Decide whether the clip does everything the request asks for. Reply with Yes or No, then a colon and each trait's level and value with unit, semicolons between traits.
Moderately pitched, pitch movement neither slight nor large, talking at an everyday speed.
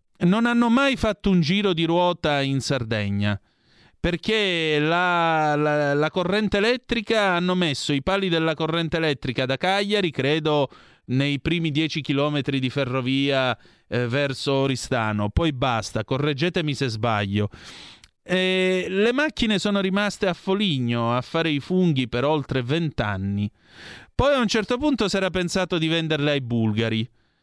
No: medium, 155 Hz; wide, 5.9 semitones; average, 145 wpm